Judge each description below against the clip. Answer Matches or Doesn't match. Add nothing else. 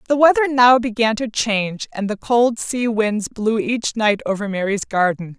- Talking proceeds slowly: Doesn't match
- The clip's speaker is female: Matches